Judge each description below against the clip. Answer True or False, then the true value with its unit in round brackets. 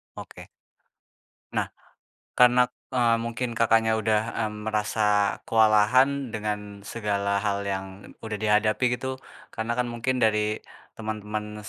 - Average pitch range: False (1.7 semitones)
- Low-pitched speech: True (110 Hz)